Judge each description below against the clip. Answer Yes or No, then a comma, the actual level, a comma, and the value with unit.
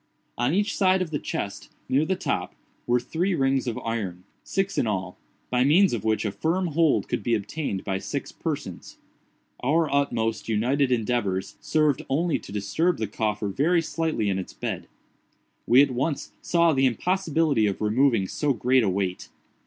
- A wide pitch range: Yes, wide, 6.8 semitones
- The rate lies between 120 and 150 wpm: No, average, 170 wpm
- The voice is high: No, low, 130 Hz